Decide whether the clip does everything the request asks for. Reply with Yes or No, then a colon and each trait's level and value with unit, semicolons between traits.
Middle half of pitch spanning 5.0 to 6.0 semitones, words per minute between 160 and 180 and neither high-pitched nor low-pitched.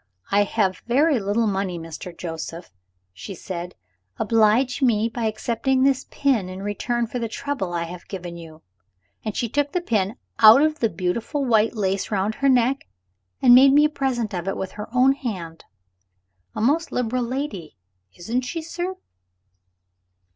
No: wide, 5.5 semitones; average, 165 wpm; high, 225 Hz